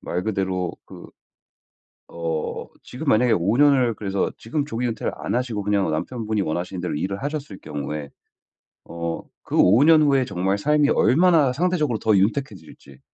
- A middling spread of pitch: No, wide, 6.9 semitones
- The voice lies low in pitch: Yes, low, 110 Hz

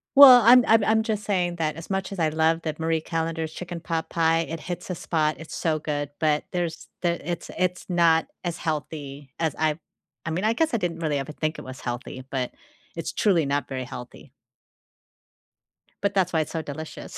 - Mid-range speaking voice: Yes, medium, 165 Hz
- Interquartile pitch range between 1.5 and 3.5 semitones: Yes, average, 2.7 semitones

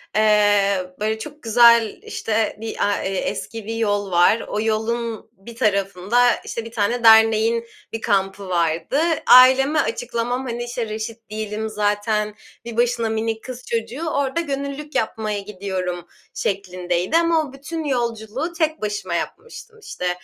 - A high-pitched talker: Yes, high, 225 Hz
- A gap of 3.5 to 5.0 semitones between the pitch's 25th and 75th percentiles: No, average, 3.1 semitones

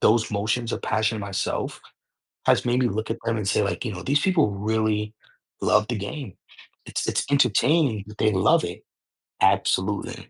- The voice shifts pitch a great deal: No, average, 2.7 semitones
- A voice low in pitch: Yes, low, 110 Hz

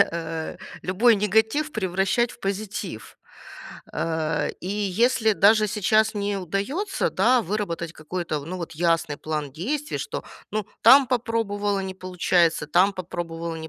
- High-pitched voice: Yes, high, 195 Hz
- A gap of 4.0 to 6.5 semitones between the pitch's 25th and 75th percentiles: Yes, average, 4.6 semitones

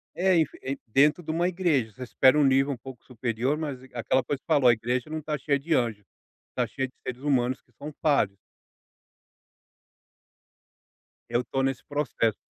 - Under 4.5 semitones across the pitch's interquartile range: Yes, average, 3.4 semitones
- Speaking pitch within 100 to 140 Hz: Yes, low, 135 Hz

